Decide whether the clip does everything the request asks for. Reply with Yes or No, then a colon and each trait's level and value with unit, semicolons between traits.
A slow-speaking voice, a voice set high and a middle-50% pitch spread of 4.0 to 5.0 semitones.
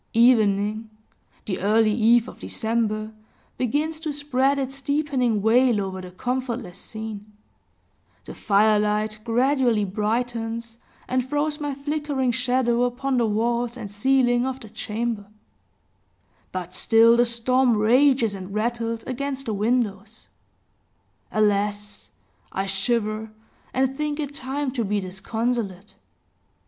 No: slow, 120 wpm; high, 235 Hz; average, 3.5 semitones